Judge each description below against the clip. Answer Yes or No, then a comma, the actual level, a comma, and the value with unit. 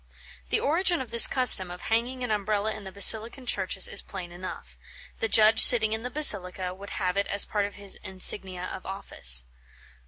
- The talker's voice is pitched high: Yes, high, 205 Hz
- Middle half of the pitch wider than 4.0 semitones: No, average, 3.3 semitones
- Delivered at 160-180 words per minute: No, average, 190 wpm